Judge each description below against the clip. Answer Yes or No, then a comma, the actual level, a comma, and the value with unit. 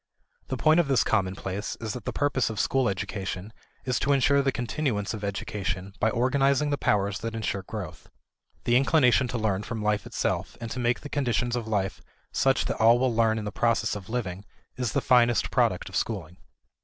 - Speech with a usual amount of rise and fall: Yes, average, 3.9 semitones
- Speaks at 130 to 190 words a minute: No, average, 200 wpm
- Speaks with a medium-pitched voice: No, low, 115 Hz